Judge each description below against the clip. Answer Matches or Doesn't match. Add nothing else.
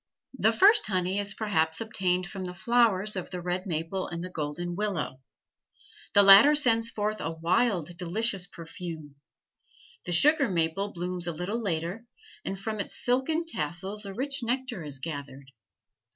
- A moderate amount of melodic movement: Matches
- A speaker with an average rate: Matches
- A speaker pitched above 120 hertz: Matches